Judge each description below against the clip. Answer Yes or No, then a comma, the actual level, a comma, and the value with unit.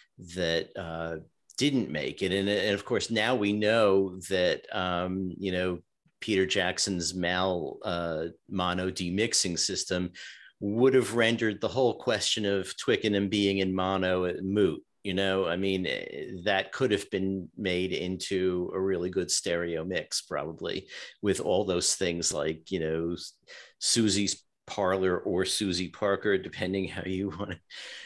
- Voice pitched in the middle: No, very low, 95 Hz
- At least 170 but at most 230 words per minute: No, average, 145 wpm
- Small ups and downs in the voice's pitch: Yes, narrow, 1.7 semitones